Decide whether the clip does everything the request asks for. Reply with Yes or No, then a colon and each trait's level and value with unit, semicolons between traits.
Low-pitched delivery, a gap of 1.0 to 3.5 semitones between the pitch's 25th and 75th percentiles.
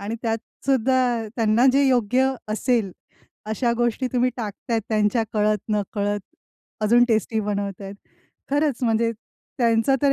No: high, 230 Hz; average, 3.0 semitones